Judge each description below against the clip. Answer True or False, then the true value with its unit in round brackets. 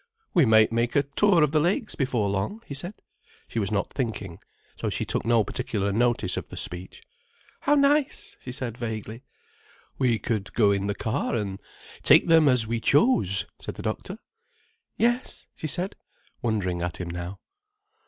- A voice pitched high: False (115 Hz)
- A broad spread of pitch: True (6.8 semitones)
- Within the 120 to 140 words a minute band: False (175 wpm)